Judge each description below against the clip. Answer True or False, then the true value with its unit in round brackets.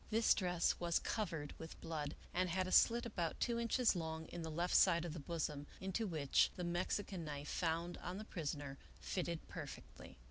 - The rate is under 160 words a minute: False (185 wpm)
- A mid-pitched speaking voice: True (170 Hz)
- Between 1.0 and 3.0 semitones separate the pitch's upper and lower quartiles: True (2.6 semitones)